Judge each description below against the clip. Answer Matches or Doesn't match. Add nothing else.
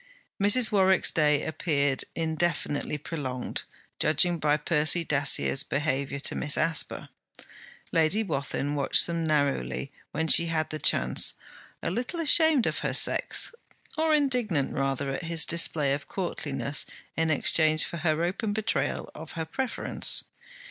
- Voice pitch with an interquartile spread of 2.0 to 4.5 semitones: Matches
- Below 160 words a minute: Matches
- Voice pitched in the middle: Matches